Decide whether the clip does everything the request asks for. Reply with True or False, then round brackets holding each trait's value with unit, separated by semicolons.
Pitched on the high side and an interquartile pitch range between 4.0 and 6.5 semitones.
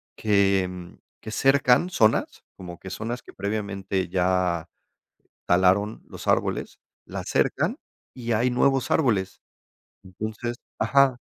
False (105 Hz; 4.6 semitones)